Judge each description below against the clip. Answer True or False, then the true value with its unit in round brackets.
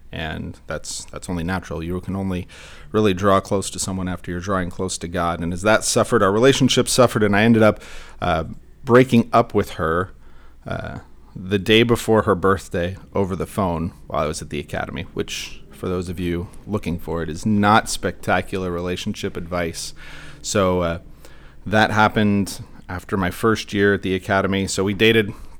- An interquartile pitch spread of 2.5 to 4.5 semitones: True (3.4 semitones)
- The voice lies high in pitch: False (95 Hz)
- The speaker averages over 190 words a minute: False (180 wpm)